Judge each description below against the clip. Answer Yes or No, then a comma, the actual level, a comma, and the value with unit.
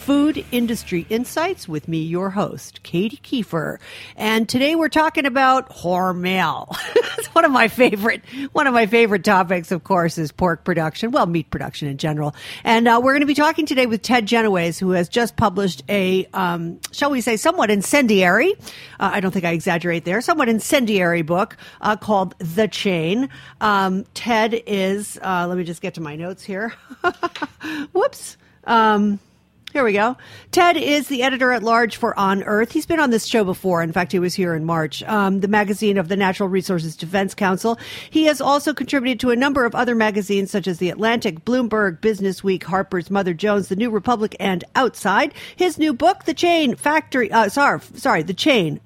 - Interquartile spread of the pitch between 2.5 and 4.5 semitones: No, wide, 5.5 semitones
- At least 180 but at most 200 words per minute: Yes, average, 190 wpm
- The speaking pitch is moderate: No, high, 210 Hz